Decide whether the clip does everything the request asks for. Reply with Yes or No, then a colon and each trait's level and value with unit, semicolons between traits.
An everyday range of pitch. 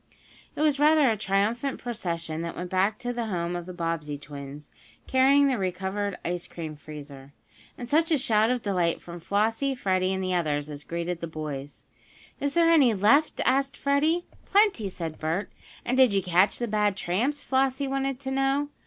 No: wide, 7.9 semitones